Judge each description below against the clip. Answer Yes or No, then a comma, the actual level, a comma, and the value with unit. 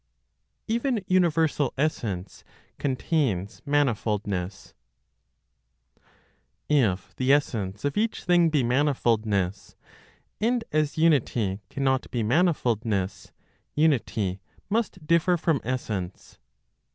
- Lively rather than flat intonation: Yes, wide, 7.4 semitones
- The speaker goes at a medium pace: No, slow, 85 wpm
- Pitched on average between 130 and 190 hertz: Yes, low, 135 Hz